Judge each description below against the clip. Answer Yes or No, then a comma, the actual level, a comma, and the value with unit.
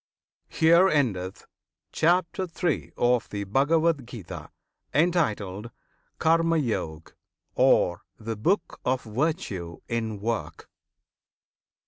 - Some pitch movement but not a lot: No, wide, 8.2 semitones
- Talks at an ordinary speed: No, slow, 90 wpm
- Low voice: Yes, low, 125 Hz